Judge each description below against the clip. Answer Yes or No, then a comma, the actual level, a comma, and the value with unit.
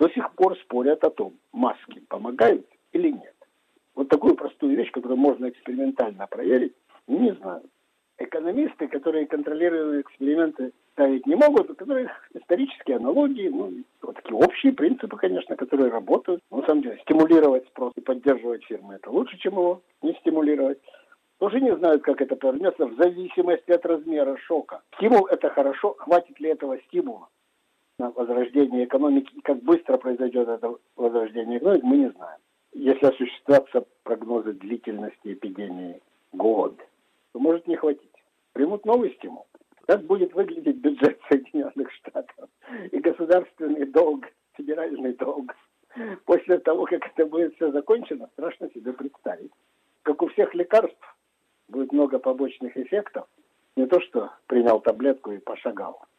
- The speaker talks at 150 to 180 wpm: No, average, 140 wpm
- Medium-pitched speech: Yes, medium, 160 Hz